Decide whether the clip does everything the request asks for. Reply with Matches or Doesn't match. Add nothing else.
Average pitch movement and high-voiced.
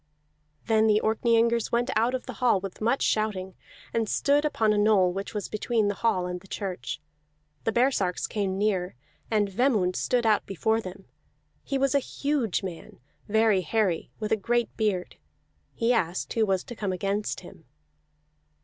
Matches